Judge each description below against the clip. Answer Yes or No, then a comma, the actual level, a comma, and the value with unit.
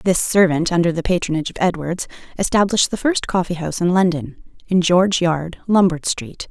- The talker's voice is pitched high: No, medium, 175 Hz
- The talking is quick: No, average, 175 wpm